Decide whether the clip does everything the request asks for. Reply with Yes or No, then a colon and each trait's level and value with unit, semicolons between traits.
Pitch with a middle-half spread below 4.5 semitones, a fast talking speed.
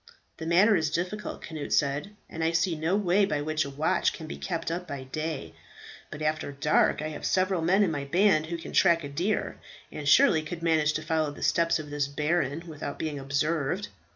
Yes: average, 2.8 semitones; fast, 210 wpm